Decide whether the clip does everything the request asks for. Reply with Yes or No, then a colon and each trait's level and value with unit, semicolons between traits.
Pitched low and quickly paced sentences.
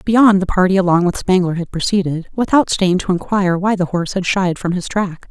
No: medium, 185 Hz; fast, 215 wpm